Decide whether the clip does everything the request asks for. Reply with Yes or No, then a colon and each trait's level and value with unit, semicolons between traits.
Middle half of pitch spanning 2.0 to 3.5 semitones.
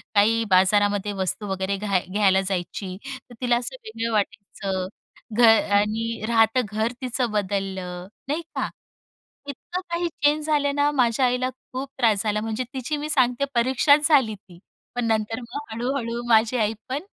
No: average, 4.2 semitones